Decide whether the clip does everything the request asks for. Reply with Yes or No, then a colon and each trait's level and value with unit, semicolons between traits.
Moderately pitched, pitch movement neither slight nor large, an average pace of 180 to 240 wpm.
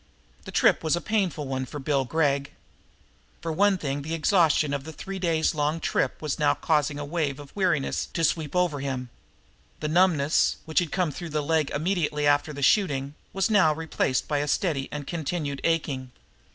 Yes: medium, 155 Hz; average, 3.0 semitones; average, 190 wpm